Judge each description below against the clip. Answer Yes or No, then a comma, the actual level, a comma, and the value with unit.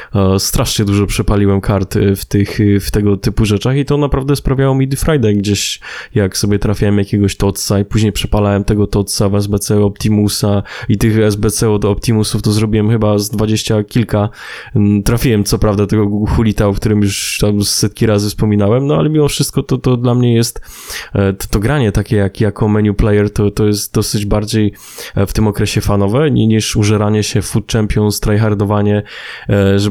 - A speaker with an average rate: No, fast, 175 wpm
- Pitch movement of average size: No, narrow, 1.5 semitones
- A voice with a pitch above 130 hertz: No, low, 105 Hz